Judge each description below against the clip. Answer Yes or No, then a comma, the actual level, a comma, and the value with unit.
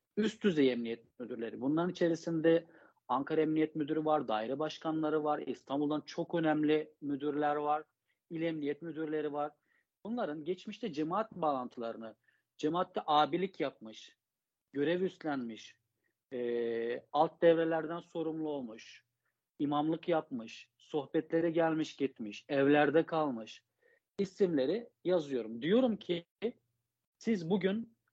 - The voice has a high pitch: No, medium, 155 Hz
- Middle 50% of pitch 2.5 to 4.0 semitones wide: Yes, average, 3.0 semitones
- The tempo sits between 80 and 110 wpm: Yes, average, 105 wpm